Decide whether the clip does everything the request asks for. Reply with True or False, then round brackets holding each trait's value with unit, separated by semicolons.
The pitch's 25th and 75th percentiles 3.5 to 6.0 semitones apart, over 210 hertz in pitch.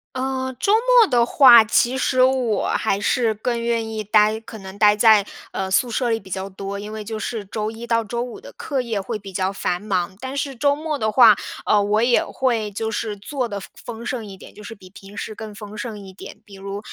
False (3.1 semitones; 220 Hz)